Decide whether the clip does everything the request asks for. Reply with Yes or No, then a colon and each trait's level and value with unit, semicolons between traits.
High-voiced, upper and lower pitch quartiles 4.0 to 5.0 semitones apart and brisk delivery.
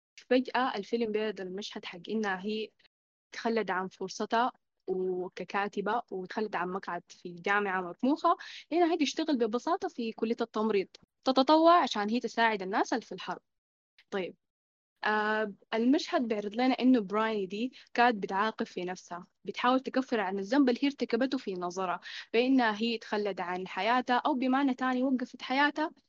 Yes: high, 225 Hz; average, 4.7 semitones; fast, 145 wpm